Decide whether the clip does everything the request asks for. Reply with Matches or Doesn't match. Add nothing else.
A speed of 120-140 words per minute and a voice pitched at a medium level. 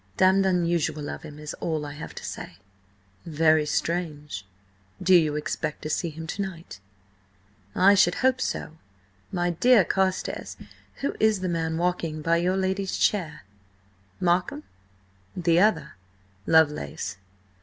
Matches